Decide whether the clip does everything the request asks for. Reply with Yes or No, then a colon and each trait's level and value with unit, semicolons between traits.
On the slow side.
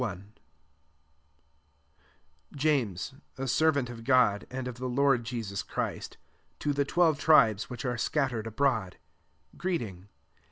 Yes: slow, 120 wpm